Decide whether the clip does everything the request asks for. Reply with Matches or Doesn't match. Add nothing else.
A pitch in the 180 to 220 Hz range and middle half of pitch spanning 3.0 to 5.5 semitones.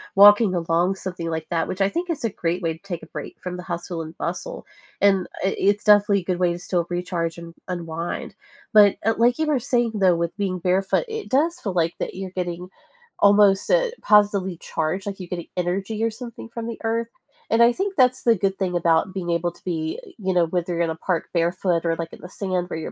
Matches